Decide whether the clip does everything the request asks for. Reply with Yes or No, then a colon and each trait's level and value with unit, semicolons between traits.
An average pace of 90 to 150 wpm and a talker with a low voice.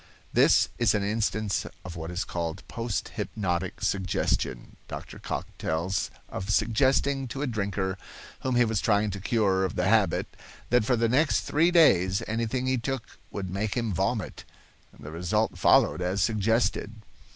No: average, 160 wpm; low, 105 Hz